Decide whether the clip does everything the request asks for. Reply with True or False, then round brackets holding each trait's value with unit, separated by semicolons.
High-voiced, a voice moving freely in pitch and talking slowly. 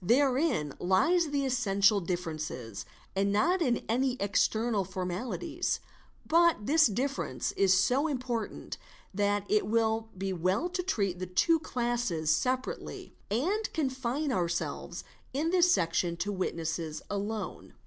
True (220 Hz; 6.7 semitones; 130 wpm)